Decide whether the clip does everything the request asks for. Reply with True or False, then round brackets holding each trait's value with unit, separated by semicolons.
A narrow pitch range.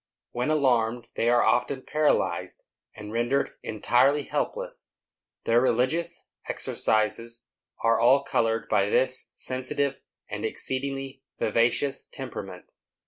False (3.2 semitones)